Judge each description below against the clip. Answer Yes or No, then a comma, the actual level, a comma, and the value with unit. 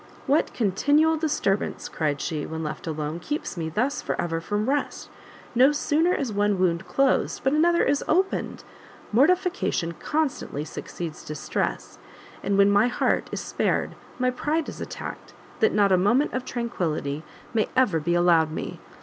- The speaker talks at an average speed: Yes, average, 160 wpm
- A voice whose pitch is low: No, high, 210 Hz